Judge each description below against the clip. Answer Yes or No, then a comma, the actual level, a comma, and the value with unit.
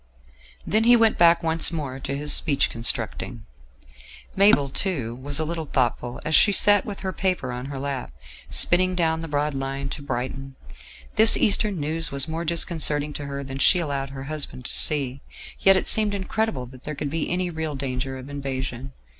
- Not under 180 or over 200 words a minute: Yes, average, 190 wpm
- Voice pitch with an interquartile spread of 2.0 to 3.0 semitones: No, average, 4.1 semitones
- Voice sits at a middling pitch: Yes, medium, 145 Hz